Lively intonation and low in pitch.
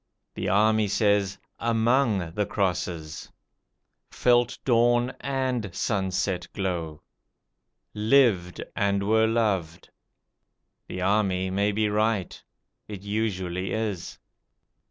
No: average, 3.3 semitones; low, 100 Hz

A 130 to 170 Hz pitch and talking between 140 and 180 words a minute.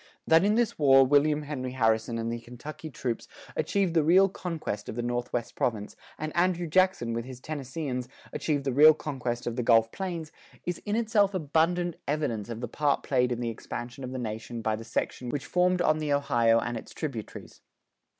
No: medium, 140 Hz; average, 195 wpm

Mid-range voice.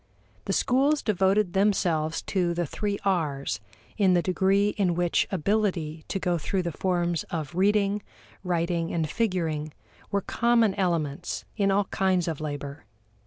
Yes: medium, 180 Hz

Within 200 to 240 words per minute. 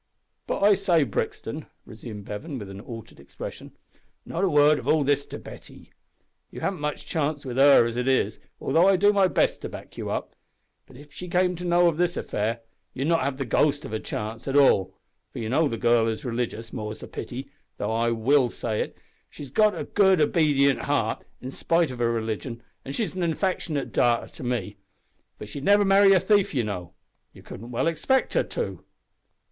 Yes: fast, 205 wpm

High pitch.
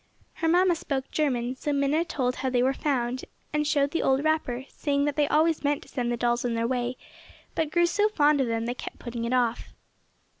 Yes: very high, 275 Hz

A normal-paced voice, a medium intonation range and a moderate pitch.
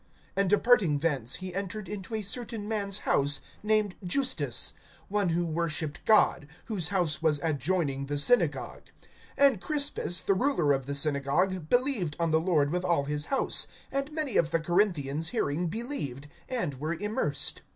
No: average, 160 wpm; wide, 6.2 semitones; medium, 175 Hz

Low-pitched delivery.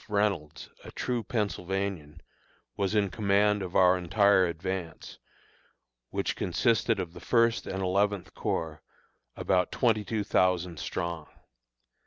Yes: very low, 95 Hz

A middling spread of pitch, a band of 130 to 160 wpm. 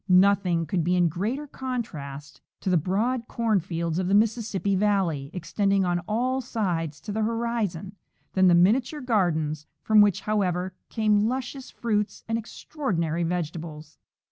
Yes: average, 4.7 semitones; average, 145 wpm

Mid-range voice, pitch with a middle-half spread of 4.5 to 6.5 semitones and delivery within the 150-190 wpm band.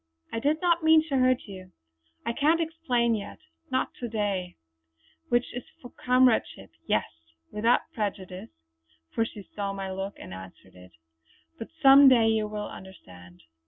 No: high, 225 Hz; average, 5.2 semitones; average, 160 wpm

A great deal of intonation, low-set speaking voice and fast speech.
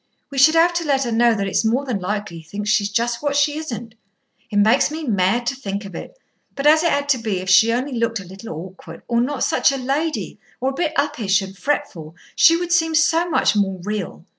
No: wide, 6.5 semitones; high, 235 Hz; fast, 240 wpm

